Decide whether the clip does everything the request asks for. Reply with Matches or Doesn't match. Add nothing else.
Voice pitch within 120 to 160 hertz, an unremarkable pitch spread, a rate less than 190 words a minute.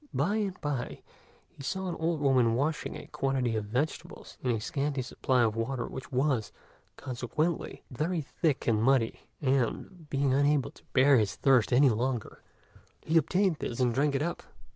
Matches